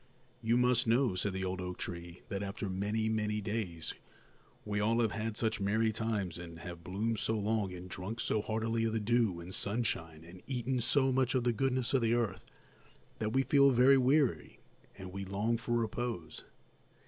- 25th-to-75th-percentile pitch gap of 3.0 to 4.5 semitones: Yes, average, 3.9 semitones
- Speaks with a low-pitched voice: Yes, low, 110 Hz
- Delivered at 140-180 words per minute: No, average, 190 wpm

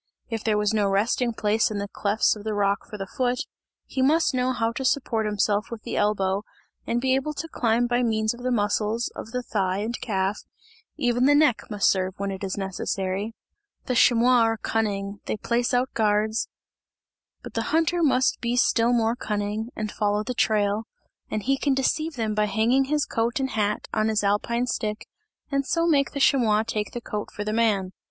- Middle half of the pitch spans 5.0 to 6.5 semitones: No, average, 3.1 semitones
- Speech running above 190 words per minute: Yes, fast, 205 wpm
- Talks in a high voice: Yes, high, 225 Hz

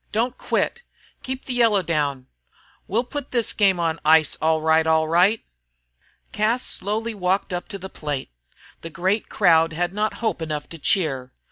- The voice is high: No, medium, 180 Hz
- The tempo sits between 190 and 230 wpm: No, average, 165 wpm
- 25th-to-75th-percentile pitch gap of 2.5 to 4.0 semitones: No, average, 5.2 semitones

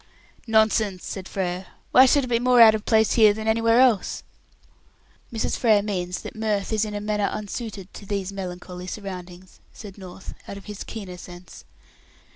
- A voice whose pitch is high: Yes, high, 205 Hz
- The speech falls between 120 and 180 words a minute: Yes, average, 175 wpm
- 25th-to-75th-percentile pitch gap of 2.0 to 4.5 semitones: Yes, average, 2.8 semitones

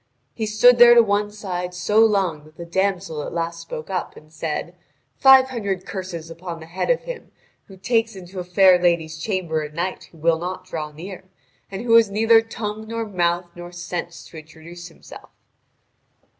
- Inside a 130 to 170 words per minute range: No, average, 185 wpm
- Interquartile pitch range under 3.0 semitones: No, average, 3.9 semitones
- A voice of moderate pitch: Yes, medium, 180 Hz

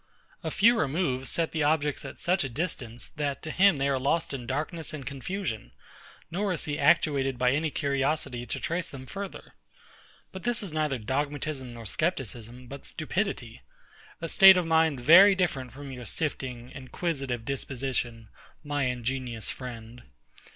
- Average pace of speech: Yes, average, 160 wpm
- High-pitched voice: No, medium, 140 Hz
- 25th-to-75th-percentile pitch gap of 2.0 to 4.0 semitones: No, average, 4.4 semitones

